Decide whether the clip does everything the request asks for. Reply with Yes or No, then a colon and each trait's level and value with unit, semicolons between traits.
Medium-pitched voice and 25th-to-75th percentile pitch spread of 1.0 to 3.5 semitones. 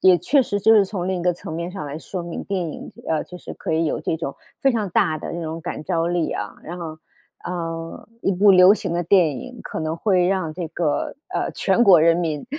Yes: medium, 175 Hz; average, 2.8 semitones